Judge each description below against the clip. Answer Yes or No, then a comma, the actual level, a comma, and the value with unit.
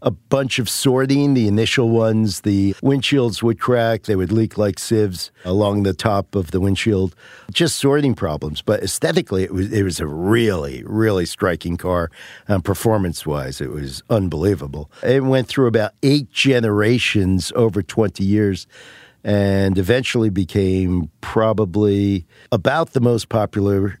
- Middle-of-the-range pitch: No, low, 105 Hz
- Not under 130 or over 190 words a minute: Yes, average, 150 wpm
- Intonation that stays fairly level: No, average, 3.5 semitones